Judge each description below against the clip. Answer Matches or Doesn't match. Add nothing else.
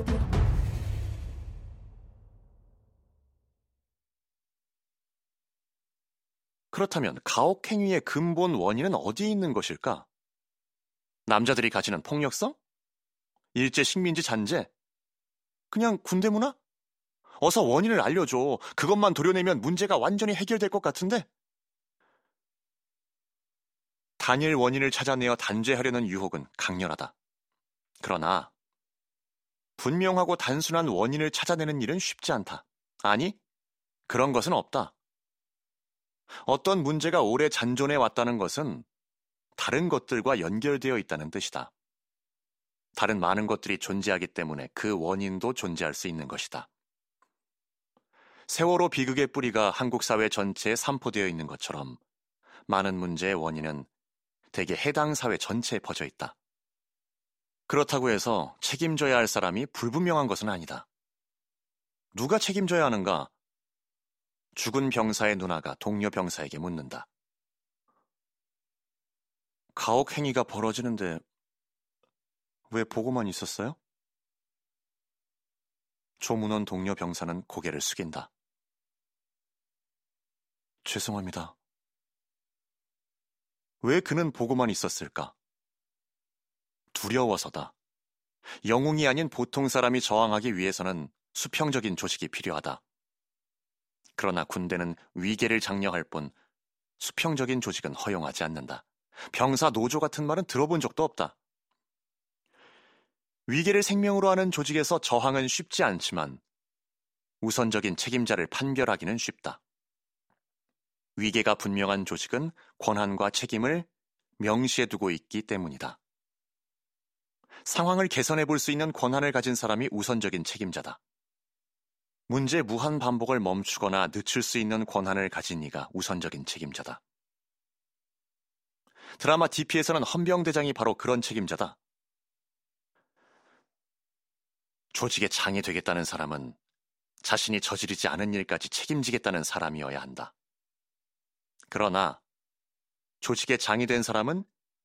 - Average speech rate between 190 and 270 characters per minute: Matches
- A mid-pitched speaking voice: Doesn't match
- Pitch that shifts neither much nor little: Doesn't match